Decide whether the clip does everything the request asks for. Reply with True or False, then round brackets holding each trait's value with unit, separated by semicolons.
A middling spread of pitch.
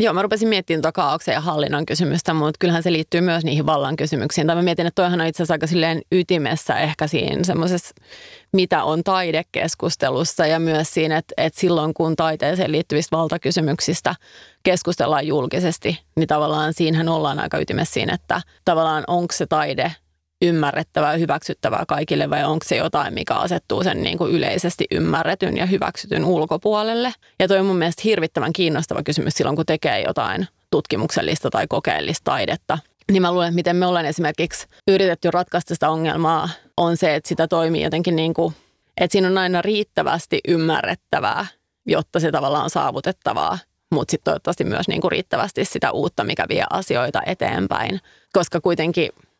False (2.1 semitones)